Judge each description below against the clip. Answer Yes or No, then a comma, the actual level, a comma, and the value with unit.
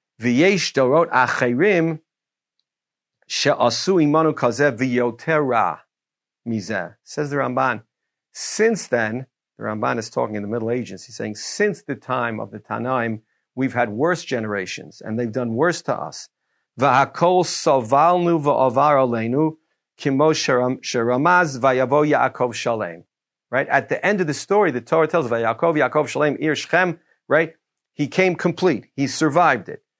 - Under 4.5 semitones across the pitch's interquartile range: No, average, 5.0 semitones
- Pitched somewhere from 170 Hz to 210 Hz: No, medium, 140 Hz